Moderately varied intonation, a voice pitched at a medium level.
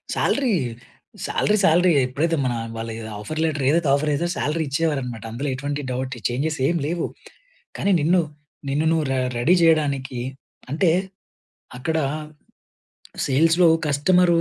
Yes: average, 3.6 semitones; medium, 150 Hz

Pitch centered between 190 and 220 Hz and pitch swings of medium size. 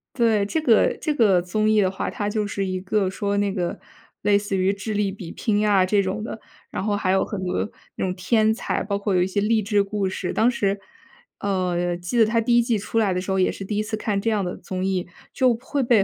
No: high, 205 Hz; narrow, 2.3 semitones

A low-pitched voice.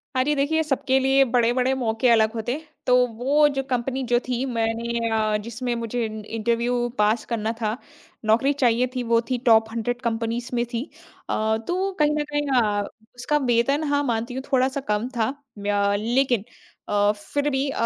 No: high, 240 Hz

